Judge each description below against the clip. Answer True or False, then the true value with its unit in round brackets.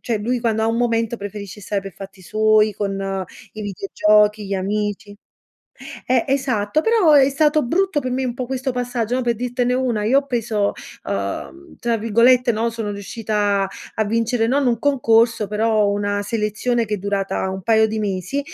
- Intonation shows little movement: False (3.3 semitones)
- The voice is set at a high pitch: True (225 Hz)